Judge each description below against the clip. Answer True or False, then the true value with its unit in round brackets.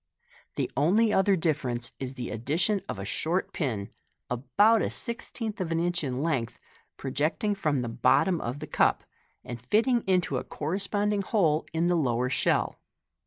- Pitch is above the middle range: False (160 Hz)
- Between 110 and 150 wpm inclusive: False (165 wpm)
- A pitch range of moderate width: False (7.3 semitones)